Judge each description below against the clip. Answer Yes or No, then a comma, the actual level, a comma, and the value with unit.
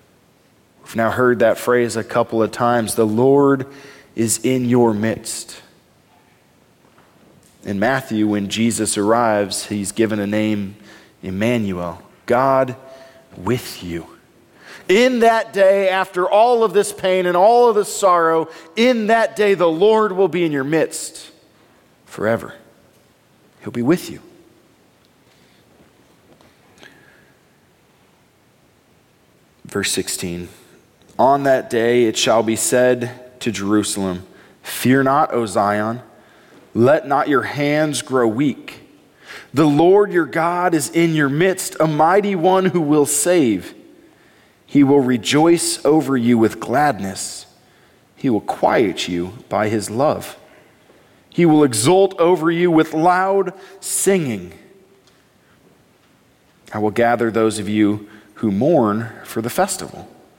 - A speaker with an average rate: No, slow, 125 wpm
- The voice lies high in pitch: No, low, 135 Hz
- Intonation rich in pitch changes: Yes, wide, 7.9 semitones